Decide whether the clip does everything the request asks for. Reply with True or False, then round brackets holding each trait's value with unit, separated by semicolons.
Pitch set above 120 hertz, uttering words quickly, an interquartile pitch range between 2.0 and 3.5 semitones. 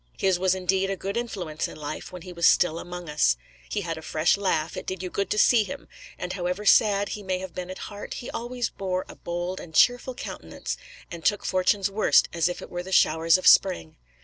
True (185 Hz; 230 wpm; 2.5 semitones)